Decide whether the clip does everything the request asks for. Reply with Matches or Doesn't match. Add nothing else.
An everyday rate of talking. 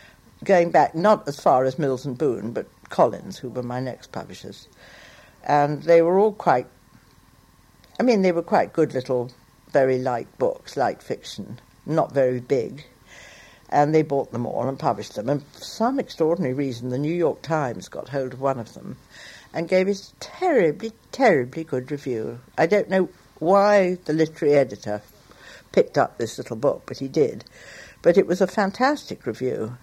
Matches